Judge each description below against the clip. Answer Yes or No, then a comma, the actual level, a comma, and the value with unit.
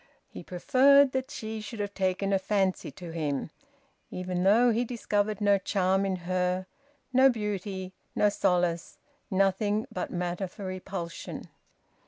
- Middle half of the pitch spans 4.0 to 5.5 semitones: No, narrow, 2.6 semitones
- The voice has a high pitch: Yes, high, 195 Hz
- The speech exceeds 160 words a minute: No, average, 140 wpm